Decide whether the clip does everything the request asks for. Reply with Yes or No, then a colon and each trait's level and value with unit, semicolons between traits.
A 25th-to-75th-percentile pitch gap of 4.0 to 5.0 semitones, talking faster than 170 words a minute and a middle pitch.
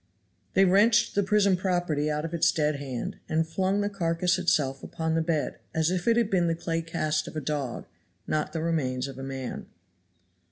No: average, 3.5 semitones; average, 200 wpm; medium, 165 Hz